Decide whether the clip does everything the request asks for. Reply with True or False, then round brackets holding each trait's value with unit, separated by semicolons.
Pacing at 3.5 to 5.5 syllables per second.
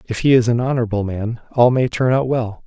False (5.8 syllables/s)